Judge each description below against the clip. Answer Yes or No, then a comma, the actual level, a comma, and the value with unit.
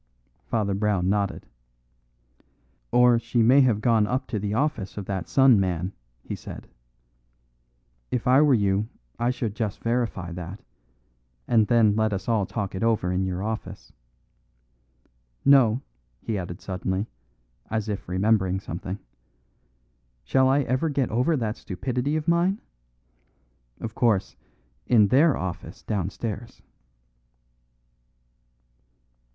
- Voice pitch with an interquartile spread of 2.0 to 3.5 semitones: No, average, 4.3 semitones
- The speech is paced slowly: Yes, slow, 125 wpm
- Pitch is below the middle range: Yes, low, 110 Hz